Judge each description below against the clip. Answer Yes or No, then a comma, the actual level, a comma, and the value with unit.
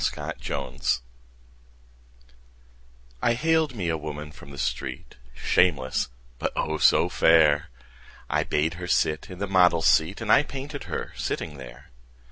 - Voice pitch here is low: Yes, very low, 80 Hz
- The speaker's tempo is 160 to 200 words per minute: No, average, 140 wpm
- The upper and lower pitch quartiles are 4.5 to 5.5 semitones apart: Yes, average, 5.0 semitones